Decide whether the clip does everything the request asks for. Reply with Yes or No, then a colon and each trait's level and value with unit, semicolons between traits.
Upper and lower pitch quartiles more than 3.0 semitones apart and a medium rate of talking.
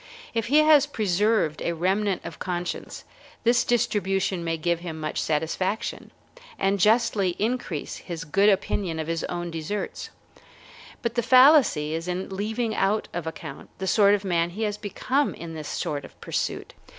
Yes: average, 4.5 semitones; average, 165 wpm